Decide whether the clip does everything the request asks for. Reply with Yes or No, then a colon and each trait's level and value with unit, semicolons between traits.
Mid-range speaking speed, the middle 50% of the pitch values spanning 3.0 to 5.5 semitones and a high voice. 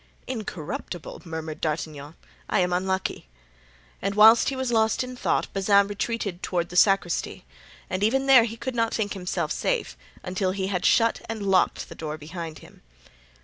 Yes: average, 165 wpm; average, 4.5 semitones; high, 195 Hz